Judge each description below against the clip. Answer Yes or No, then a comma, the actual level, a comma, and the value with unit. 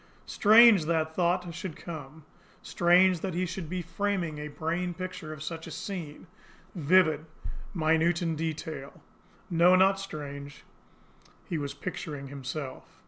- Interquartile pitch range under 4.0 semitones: Yes, average, 3.1 semitones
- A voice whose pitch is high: No, medium, 165 Hz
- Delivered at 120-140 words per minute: Yes, slow, 135 wpm